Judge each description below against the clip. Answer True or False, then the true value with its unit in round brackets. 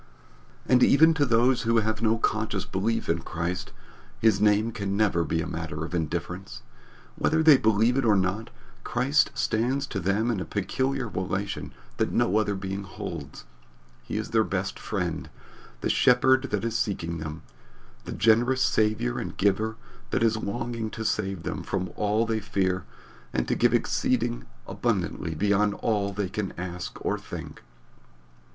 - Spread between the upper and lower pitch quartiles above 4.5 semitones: False (3.6 semitones)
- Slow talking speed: False (165 wpm)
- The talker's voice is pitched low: True (105 Hz)